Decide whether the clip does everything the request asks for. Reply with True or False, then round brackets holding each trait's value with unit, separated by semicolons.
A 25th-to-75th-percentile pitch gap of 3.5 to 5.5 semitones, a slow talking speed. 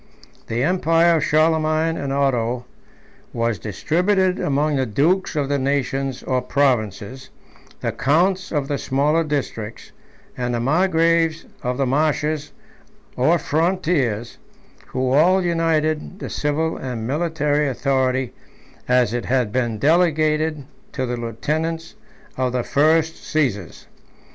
True (4.1 semitones; 125 wpm)